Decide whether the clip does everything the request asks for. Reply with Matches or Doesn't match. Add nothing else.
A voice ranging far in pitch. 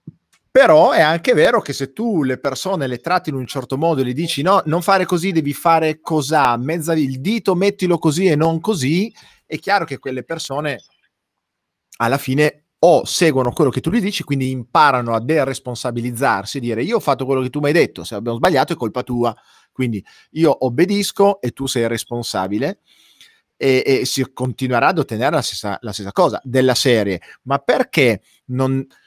Doesn't match